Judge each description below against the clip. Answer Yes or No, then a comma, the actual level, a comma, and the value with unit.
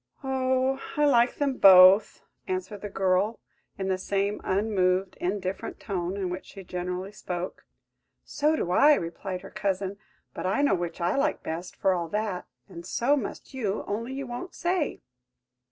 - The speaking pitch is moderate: No, high, 200 Hz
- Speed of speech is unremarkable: Yes, average, 165 wpm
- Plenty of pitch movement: Yes, wide, 5.9 semitones